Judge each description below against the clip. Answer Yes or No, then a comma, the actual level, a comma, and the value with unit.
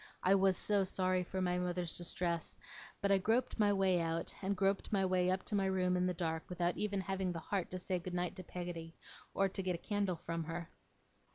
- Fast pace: Yes, fast, 225 wpm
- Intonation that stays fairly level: Yes, narrow, 1.8 semitones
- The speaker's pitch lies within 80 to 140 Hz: No, medium, 185 Hz